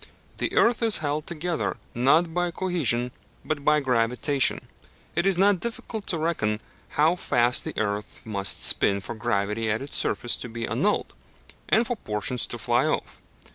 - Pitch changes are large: Yes, wide, 7.4 semitones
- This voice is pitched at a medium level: Yes, medium, 145 Hz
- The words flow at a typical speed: Yes, average, 165 wpm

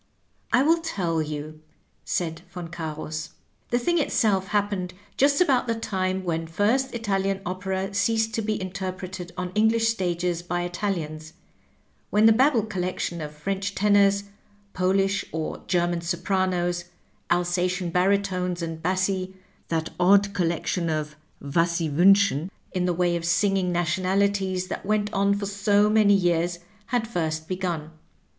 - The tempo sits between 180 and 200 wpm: No, average, 145 wpm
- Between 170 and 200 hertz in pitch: Yes, medium, 185 Hz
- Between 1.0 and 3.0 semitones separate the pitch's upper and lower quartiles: Yes, average, 2.7 semitones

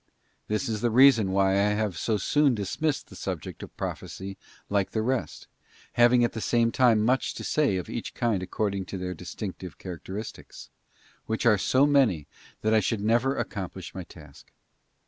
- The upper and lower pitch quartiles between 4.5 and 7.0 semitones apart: No, average, 3.9 semitones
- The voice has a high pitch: No, low, 105 Hz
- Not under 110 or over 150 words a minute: No, average, 170 wpm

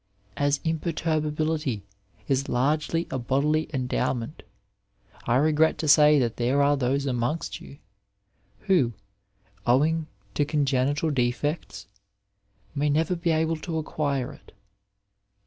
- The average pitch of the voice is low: No, medium, 145 Hz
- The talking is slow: Yes, slow, 115 wpm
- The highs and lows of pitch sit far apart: No, average, 3.1 semitones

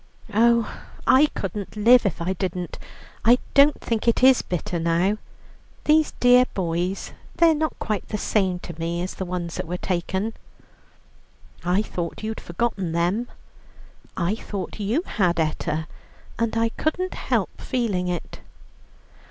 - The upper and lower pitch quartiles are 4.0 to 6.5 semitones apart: Yes, average, 5.0 semitones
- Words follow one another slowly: No, average, 145 wpm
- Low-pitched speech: No, high, 200 Hz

